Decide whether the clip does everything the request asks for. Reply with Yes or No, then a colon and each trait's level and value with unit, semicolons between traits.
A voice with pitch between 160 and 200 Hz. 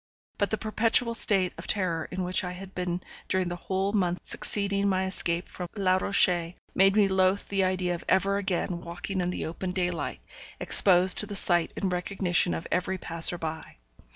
Yes: medium, 185 Hz